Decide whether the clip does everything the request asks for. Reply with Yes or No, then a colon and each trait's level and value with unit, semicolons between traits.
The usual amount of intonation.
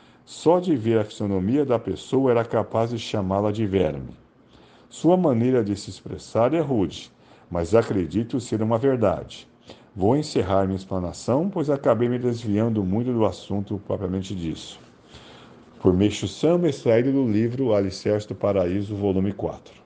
Yes: average, 3.8 semitones